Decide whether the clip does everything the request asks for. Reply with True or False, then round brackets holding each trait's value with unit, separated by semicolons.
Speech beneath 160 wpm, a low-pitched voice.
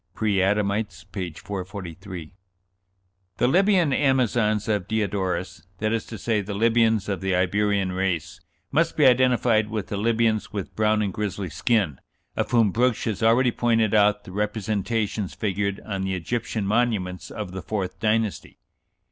True (150 wpm; 105 Hz)